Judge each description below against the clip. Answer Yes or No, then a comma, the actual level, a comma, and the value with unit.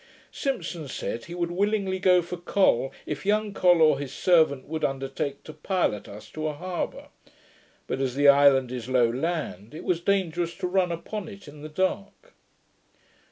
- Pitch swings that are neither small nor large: Yes, average, 5.0 semitones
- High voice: No, medium, 165 Hz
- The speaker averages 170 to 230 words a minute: Yes, average, 175 wpm